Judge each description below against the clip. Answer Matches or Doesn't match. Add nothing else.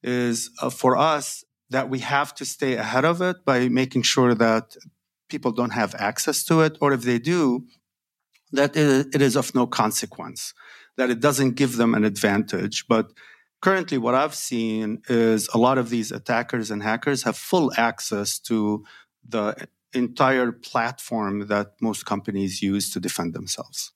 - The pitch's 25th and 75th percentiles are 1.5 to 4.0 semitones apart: Matches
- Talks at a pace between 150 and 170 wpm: Matches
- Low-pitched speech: Matches